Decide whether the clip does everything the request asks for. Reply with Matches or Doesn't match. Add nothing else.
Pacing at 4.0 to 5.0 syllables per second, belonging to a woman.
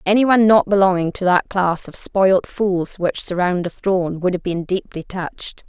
Matches